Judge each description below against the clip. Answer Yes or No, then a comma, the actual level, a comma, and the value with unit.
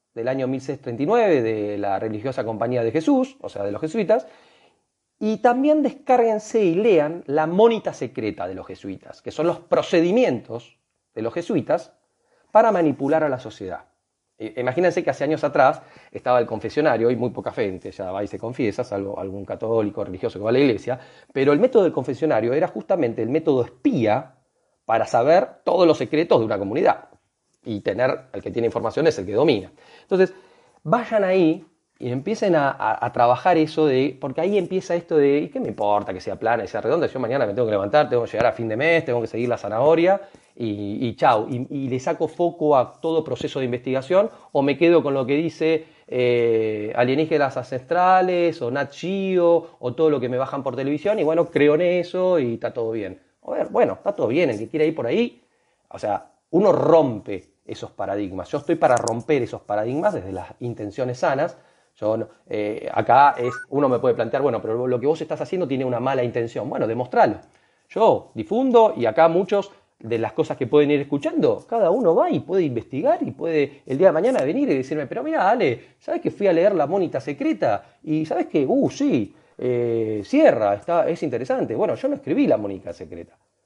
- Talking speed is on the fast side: Yes, fast, 200 wpm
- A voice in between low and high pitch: Yes, medium, 145 Hz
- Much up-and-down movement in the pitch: Yes, wide, 6.4 semitones